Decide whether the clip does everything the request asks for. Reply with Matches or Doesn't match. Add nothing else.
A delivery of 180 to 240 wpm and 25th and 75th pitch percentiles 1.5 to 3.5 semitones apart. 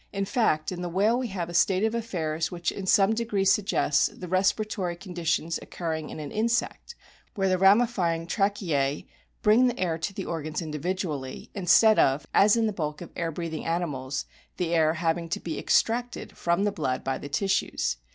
Doesn't match